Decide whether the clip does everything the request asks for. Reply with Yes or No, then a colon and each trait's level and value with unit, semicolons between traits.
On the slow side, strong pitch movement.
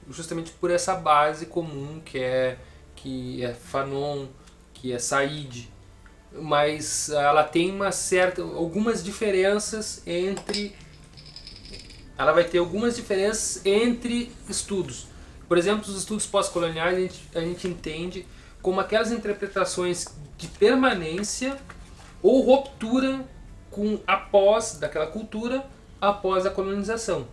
Yes: slow, 115 wpm; wide, 5.8 semitones